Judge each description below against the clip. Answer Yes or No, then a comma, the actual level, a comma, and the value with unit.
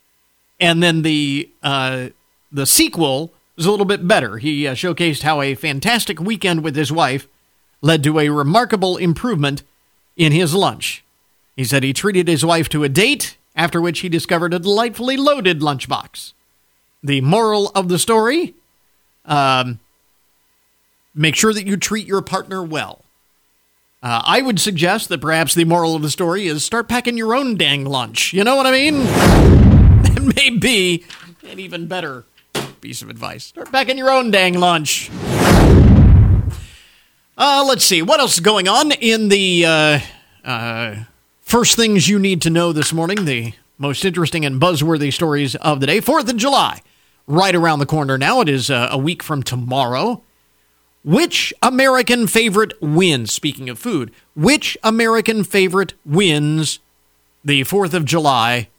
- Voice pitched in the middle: Yes, medium, 170 Hz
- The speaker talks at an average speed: Yes, average, 160 wpm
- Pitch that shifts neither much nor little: No, wide, 6.1 semitones